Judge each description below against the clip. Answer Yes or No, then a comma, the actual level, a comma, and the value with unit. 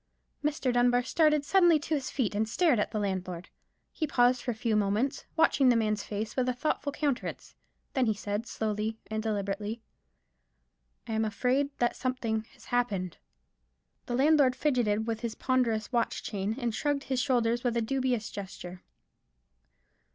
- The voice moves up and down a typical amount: Yes, average, 3.5 semitones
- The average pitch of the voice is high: Yes, high, 240 Hz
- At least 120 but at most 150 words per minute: No, average, 165 wpm